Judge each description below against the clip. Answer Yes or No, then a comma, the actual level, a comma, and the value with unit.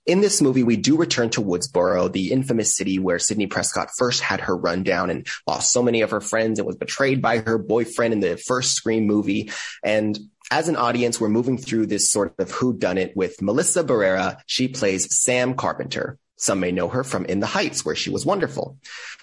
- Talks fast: Yes, fast, 210 wpm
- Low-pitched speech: Yes, low, 115 Hz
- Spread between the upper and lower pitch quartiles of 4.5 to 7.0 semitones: No, average, 3.2 semitones